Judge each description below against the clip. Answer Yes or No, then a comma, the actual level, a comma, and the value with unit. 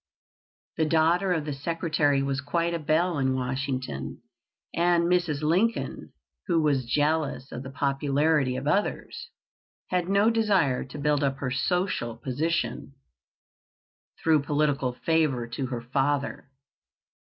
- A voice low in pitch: No, medium, 150 Hz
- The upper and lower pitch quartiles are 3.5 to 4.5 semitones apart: Yes, average, 3.8 semitones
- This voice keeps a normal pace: No, slow, 130 wpm